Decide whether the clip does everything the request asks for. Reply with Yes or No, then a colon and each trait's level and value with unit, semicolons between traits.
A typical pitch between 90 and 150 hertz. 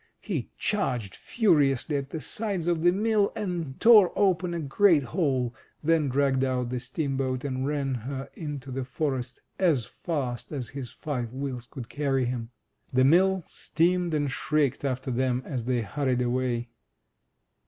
Yes: low, 135 Hz